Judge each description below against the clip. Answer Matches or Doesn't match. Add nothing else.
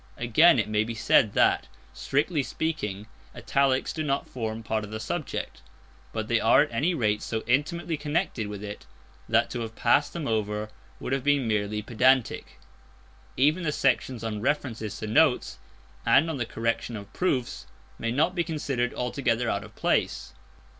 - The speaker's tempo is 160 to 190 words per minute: Matches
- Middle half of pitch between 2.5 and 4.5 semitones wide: Doesn't match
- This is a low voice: Matches